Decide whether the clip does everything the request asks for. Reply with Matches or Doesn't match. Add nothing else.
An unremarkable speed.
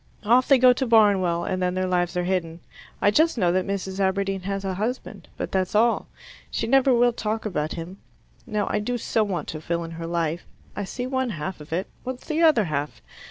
Doesn't match